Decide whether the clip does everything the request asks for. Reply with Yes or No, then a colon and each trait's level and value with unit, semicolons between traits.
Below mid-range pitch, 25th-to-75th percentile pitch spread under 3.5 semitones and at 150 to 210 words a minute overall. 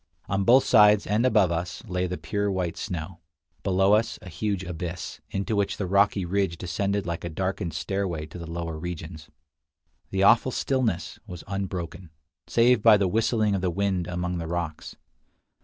Yes: very low, 95 Hz; average, 2.9 semitones; average, 175 wpm